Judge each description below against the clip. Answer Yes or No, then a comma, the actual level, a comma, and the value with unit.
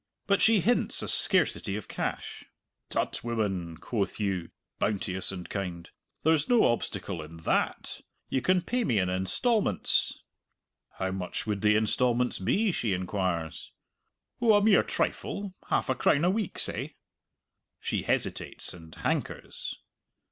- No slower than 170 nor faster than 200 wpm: No, average, 140 wpm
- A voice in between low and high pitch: No, low, 105 Hz